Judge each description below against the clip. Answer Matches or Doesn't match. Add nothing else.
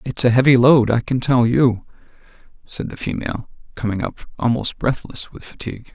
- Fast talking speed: Doesn't match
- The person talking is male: Matches